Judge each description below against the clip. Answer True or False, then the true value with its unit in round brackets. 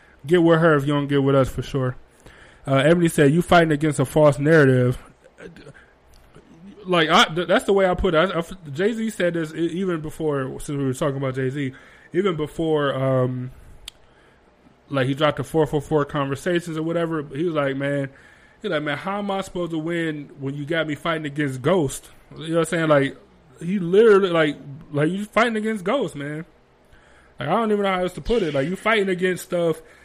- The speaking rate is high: True (210 wpm)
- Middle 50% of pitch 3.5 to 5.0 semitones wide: True (4.0 semitones)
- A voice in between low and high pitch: True (160 Hz)